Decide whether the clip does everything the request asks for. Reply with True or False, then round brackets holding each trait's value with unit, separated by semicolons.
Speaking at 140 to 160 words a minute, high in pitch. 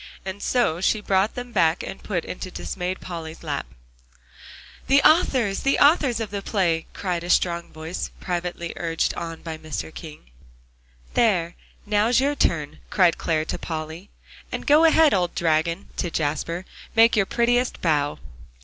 False (155 wpm; 180 Hz)